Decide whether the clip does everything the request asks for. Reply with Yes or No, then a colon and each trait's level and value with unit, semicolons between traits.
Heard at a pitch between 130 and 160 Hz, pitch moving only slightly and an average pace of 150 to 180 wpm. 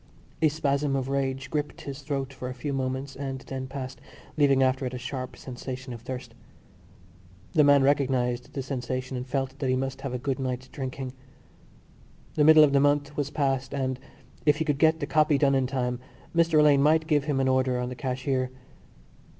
No: low, 135 Hz; narrow, 1.8 semitones; average, 200 wpm